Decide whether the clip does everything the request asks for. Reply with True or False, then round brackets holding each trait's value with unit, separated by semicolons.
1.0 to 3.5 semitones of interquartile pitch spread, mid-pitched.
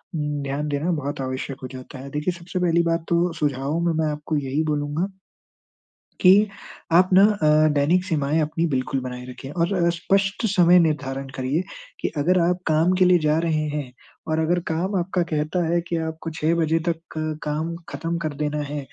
True (2.7 semitones; 155 Hz)